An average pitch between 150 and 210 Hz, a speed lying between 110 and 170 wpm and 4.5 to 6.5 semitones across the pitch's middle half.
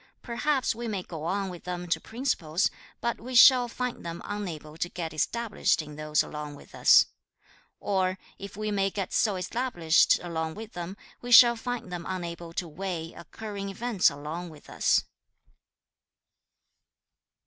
Yes: medium, 185 Hz; average, 155 wpm; average, 5.1 semitones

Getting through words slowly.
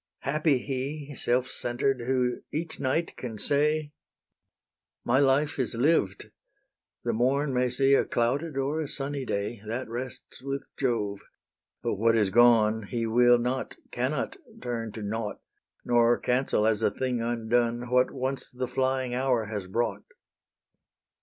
No: average, 145 wpm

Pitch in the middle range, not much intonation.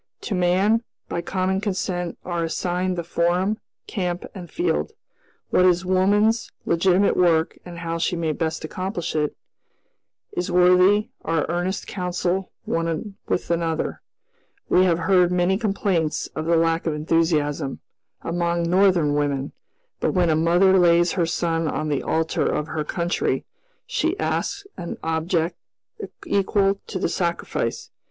Yes: medium, 175 Hz; narrow, 2.2 semitones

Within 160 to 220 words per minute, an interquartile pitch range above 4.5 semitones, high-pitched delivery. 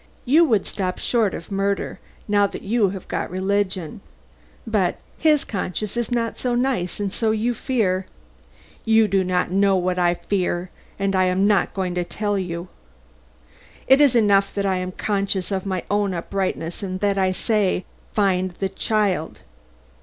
No: average, 170 wpm; narrow, 2.5 semitones; high, 195 Hz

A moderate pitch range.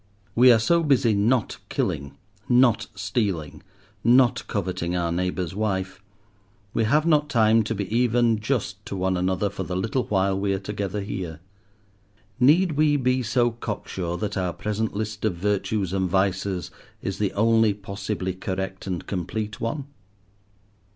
Yes: average, 3.6 semitones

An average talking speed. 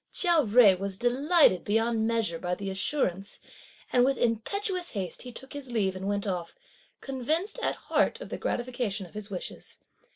Yes: average, 170 wpm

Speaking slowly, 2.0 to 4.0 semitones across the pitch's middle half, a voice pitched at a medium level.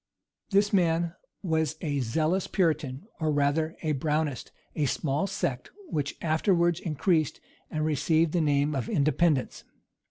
Yes: slow, 130 wpm; average, 2.7 semitones; medium, 155 Hz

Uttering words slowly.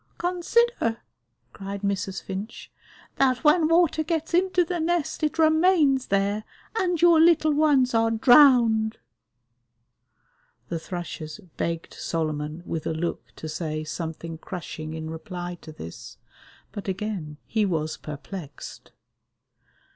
Yes: slow, 120 wpm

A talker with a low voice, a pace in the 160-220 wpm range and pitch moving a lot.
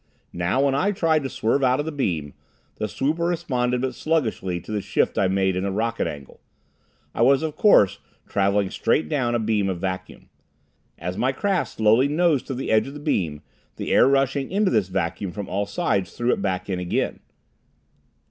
Yes: low, 115 Hz; average, 195 wpm; wide, 6.6 semitones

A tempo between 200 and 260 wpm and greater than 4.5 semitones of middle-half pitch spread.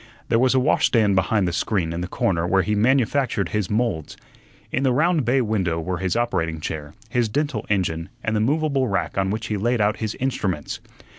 Yes: fast, 205 wpm; average, 5.2 semitones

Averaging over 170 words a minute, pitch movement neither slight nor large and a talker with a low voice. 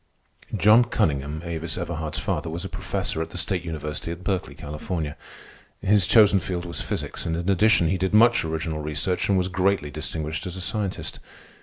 Yes: average, 180 wpm; average, 3.4 semitones; very low, 85 Hz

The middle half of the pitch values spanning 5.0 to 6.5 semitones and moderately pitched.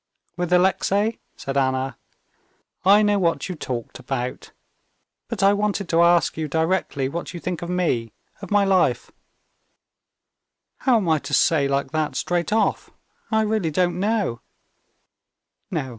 Yes: average, 5.3 semitones; medium, 175 Hz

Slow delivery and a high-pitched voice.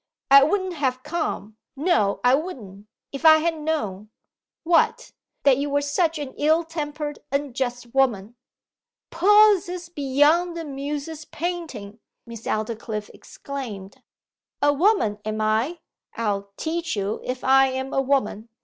Yes: slow, 130 wpm; very high, 280 Hz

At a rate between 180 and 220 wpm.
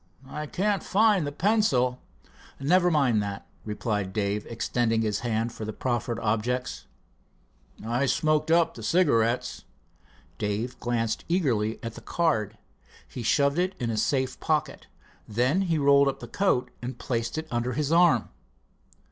No: average, 150 wpm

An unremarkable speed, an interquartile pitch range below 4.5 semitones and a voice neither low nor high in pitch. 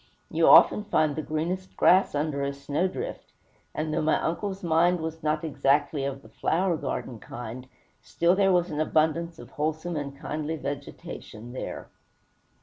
Yes: average, 155 wpm; average, 3.2 semitones; medium, 155 Hz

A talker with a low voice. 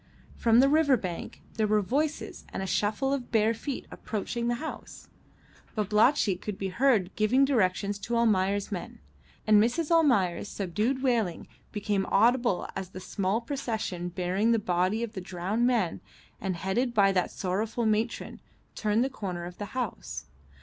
No: high, 215 Hz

